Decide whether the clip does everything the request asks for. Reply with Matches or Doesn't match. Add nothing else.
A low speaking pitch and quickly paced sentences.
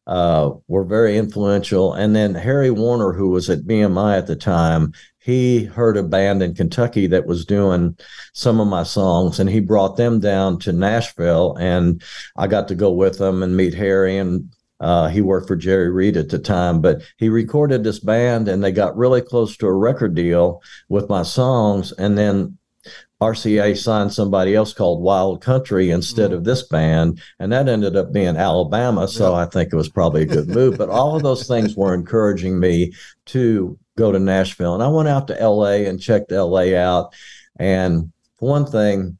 Doesn't match